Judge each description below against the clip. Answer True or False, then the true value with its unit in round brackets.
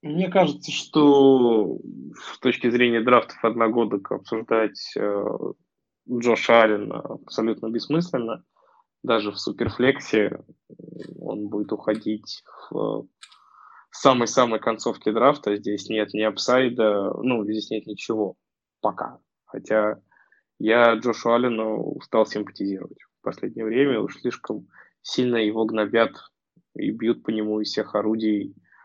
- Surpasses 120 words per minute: False (115 wpm)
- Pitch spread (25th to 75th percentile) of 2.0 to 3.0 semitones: True (2.4 semitones)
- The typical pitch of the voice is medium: False (110 Hz)